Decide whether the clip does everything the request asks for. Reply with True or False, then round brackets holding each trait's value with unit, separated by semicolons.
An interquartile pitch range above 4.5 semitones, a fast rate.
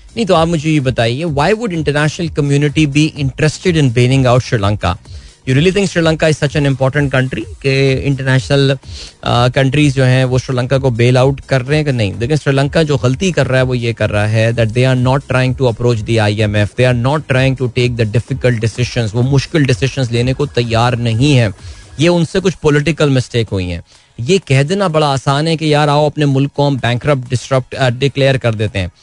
False (3.5 semitones; 220 wpm)